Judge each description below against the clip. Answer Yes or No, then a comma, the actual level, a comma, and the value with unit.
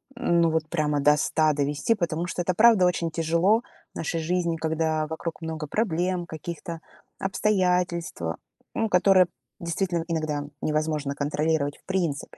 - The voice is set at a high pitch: No, medium, 165 Hz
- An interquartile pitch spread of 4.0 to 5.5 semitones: No, average, 2.7 semitones